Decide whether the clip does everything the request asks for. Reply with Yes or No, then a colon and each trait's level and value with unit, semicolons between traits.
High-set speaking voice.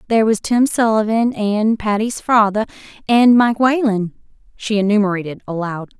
Yes: high, 215 Hz